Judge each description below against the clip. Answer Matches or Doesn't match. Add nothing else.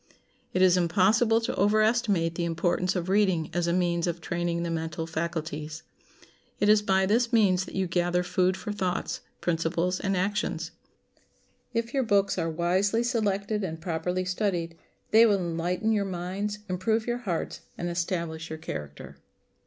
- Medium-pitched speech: Matches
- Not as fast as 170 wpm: Matches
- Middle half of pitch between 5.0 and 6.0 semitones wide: Doesn't match